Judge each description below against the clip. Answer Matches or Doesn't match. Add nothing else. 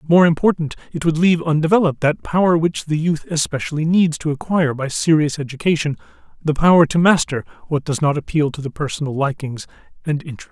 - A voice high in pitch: Doesn't match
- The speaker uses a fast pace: Doesn't match